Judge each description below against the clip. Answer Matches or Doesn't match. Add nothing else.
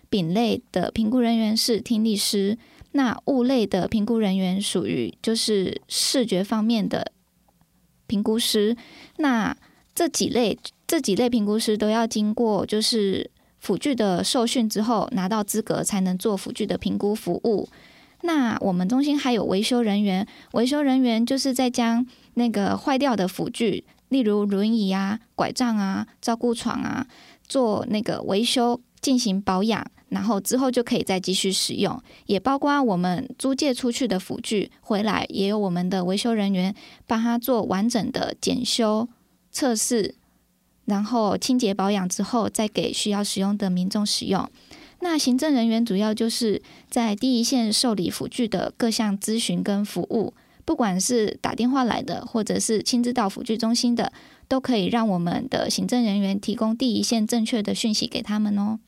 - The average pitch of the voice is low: Doesn't match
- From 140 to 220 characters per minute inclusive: Doesn't match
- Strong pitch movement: Doesn't match